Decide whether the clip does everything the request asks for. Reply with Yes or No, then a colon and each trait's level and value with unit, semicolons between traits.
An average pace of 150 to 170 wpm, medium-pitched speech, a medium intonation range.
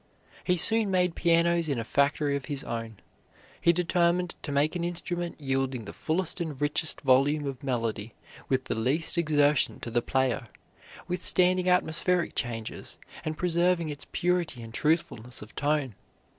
Yes: average, 155 wpm; medium, 150 Hz; average, 4.7 semitones